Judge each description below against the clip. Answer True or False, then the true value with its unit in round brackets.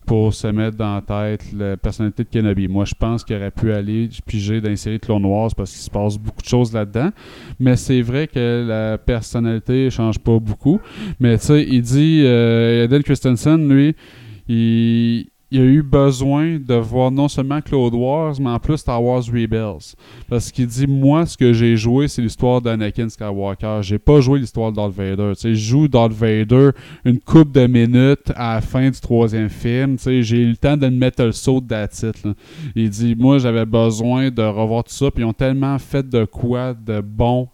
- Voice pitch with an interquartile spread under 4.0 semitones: True (3.3 semitones)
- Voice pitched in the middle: False (120 Hz)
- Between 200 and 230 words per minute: True (205 wpm)